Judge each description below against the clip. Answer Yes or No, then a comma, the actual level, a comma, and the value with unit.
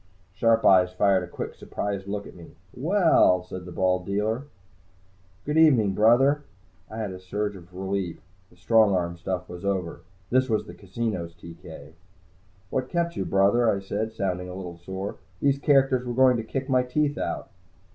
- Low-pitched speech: Yes, low, 100 Hz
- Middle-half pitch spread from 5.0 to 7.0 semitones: Yes, wide, 5.4 semitones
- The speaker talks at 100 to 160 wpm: No, average, 175 wpm